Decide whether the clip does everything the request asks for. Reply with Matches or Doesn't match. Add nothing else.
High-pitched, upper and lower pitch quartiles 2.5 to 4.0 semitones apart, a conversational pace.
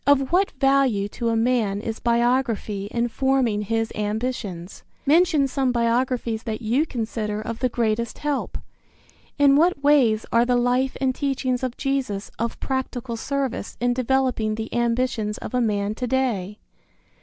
Matches